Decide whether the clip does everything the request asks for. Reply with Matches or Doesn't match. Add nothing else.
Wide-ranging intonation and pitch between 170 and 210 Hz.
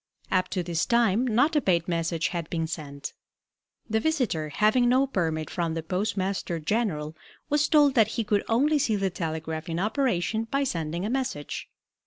Matches